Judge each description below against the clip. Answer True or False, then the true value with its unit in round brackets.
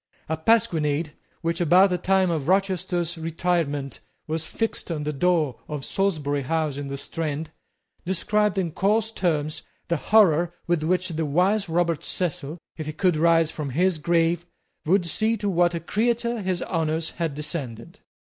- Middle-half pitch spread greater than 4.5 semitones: False (3.2 semitones)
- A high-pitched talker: False (170 Hz)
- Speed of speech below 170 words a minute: True (160 wpm)